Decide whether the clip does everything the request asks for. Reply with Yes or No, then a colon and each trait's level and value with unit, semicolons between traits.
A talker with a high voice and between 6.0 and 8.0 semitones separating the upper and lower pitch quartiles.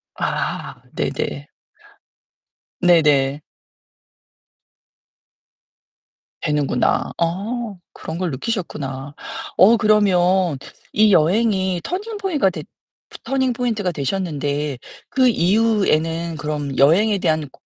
No: medium, 175 Hz; wide, 6.3 semitones